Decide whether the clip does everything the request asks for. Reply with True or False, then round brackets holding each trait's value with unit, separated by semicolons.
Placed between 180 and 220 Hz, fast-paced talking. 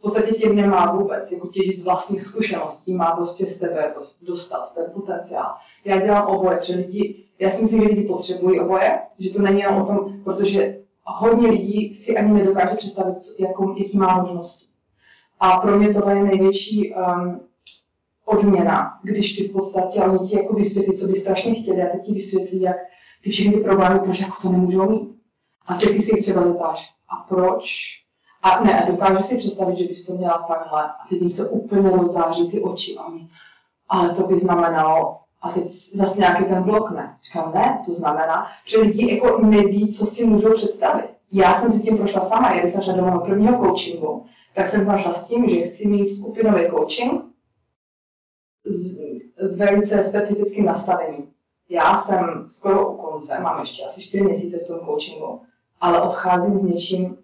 True (190 Hz; 185 wpm)